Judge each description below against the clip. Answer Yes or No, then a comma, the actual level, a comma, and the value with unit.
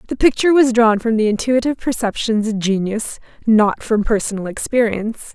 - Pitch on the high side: Yes, high, 225 Hz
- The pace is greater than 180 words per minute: No, average, 155 wpm